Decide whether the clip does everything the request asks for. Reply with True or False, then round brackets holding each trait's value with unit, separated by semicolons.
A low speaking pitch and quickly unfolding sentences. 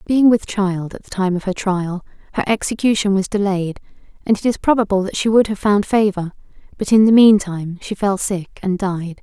False (200 Hz; 215 wpm)